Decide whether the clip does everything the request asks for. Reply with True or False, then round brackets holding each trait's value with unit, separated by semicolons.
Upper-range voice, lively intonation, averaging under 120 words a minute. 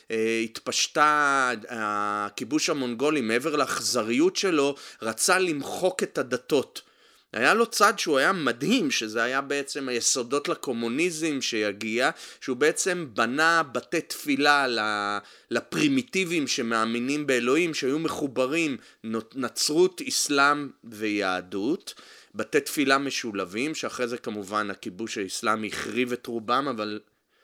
False (135 Hz; 6.8 semitones; 105 wpm)